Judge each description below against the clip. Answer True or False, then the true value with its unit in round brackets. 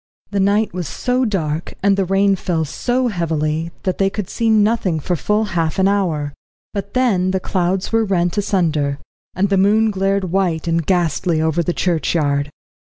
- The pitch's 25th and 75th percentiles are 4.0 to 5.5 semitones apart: False (3.5 semitones)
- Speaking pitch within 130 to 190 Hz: True (185 Hz)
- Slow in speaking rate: False (175 wpm)